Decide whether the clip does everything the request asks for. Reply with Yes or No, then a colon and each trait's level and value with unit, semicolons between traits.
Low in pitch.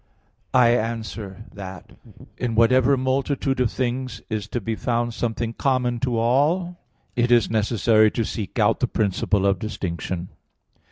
Yes: low, 115 Hz